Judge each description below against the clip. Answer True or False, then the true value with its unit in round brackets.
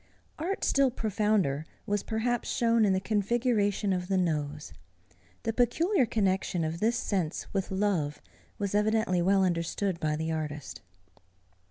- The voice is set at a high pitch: True (200 Hz)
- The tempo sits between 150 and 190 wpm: False (140 wpm)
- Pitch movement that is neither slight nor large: True (4.7 semitones)